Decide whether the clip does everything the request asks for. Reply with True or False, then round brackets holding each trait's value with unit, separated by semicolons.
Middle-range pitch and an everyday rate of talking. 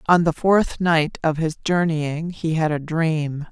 True (160 Hz; 190 wpm)